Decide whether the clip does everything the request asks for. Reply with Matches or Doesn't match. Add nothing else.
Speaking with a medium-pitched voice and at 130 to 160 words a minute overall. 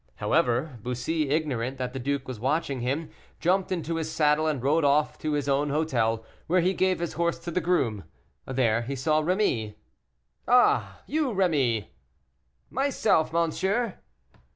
Matches